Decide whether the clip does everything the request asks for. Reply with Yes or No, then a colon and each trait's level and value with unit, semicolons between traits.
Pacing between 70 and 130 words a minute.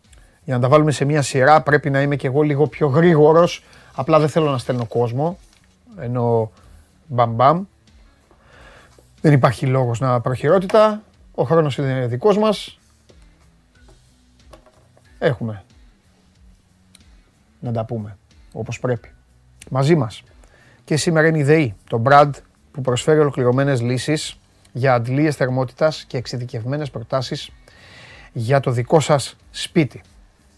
Yes: average, 125 wpm